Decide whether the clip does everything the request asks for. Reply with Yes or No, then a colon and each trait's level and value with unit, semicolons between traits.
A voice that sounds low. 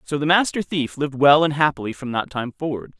No: medium, 145 Hz